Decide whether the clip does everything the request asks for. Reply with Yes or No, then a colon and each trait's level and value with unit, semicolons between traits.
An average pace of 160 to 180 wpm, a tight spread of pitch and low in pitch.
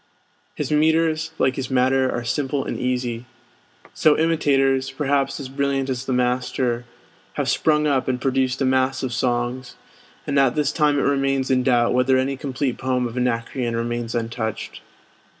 Yes: average, 165 wpm; narrow, 1.9 semitones; low, 130 Hz